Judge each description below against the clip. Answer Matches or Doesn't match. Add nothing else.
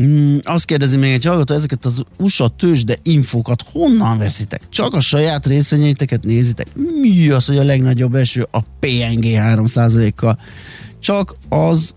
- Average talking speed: Matches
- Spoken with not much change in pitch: Doesn't match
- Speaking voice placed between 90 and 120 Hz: Doesn't match